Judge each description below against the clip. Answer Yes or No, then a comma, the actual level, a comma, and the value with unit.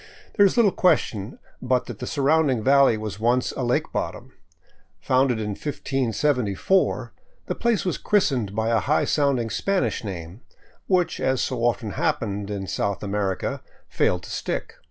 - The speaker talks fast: No, average, 155 wpm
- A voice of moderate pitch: No, low, 125 Hz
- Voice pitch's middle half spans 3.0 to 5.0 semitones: No, wide, 5.6 semitones